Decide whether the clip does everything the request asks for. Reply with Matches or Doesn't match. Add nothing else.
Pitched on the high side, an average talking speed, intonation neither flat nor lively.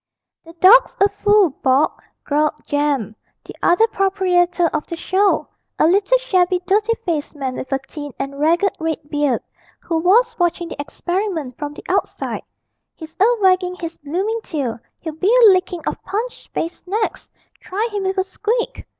Matches